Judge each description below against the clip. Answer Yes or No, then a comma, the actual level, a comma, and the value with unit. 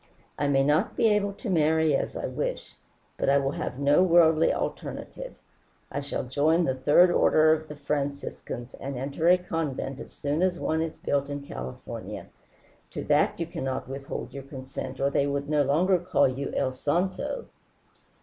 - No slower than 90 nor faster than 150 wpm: No, average, 180 wpm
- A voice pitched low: No, medium, 145 Hz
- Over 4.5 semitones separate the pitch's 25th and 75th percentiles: No, average, 3.4 semitones